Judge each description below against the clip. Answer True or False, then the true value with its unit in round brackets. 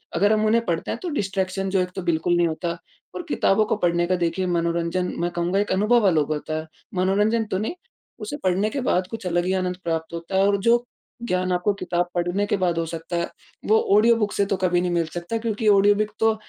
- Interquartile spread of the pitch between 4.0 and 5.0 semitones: False (3.4 semitones)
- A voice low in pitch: False (185 Hz)